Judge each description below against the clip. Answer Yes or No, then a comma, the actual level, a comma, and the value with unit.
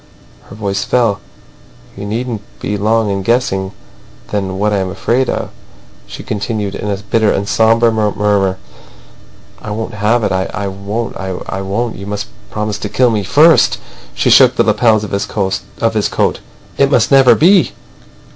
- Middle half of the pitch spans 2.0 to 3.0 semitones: Yes, narrow, 2.5 semitones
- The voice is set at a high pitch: No, low, 105 Hz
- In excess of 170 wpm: No, average, 165 wpm